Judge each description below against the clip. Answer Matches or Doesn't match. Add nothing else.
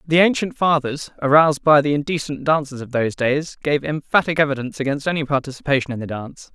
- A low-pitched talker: Doesn't match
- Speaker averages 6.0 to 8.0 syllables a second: Matches